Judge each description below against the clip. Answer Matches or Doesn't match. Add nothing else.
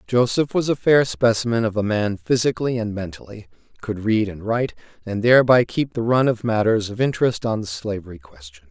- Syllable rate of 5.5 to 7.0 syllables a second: Matches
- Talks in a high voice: Doesn't match